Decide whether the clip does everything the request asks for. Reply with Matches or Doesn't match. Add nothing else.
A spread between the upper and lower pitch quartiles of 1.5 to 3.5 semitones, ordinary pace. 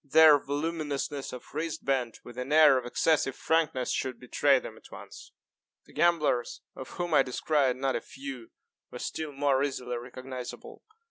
Matches